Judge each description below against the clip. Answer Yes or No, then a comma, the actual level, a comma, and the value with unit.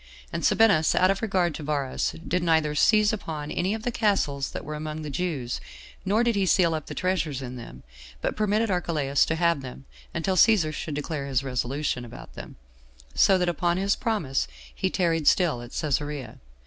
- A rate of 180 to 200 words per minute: Yes, average, 195 wpm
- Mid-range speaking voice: Yes, medium, 160 Hz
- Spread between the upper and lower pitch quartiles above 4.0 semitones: Yes, average, 4.9 semitones